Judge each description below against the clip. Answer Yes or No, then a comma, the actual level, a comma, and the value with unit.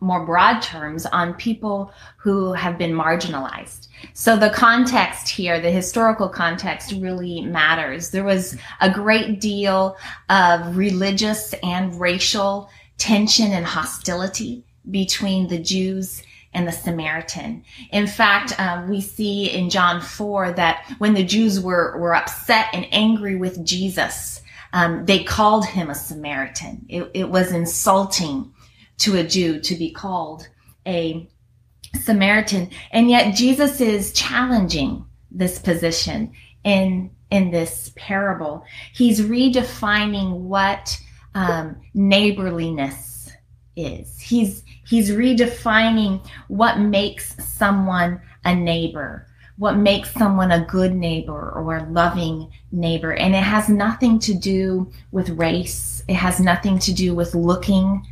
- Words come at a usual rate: No, slow, 125 wpm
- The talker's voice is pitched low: No, medium, 185 Hz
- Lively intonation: No, average, 3.3 semitones